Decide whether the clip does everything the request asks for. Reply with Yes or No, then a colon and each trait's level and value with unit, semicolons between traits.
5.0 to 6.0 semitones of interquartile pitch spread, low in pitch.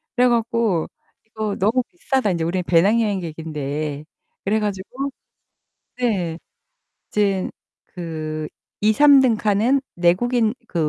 No: wide, 5.6 semitones; high, 205 Hz